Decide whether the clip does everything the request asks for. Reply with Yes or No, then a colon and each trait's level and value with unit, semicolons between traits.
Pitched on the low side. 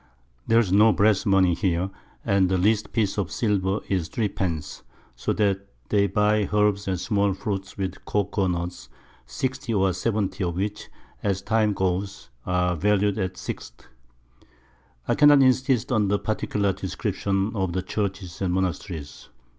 Yes: low, 100 Hz